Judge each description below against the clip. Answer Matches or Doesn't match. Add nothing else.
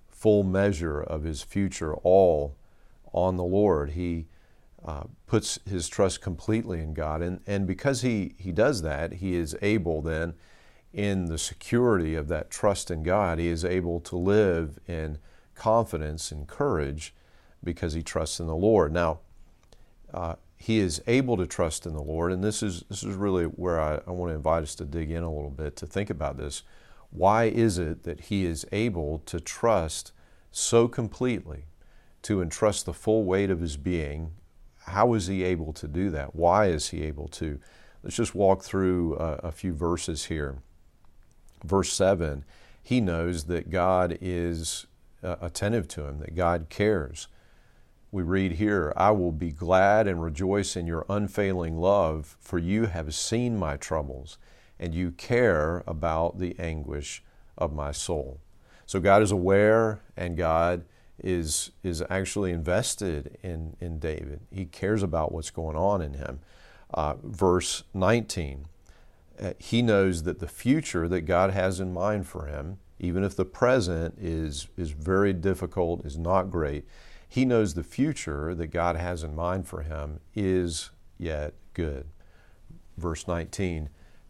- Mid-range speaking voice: Doesn't match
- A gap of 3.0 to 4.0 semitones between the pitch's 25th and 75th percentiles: Matches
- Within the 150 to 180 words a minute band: Matches